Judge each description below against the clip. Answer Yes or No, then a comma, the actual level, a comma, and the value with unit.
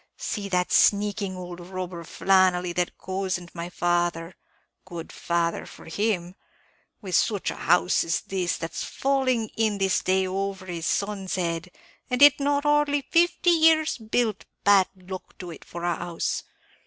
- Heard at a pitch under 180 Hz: No, medium, 185 Hz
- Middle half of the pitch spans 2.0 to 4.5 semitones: Yes, average, 3.8 semitones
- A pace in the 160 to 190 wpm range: No, average, 150 wpm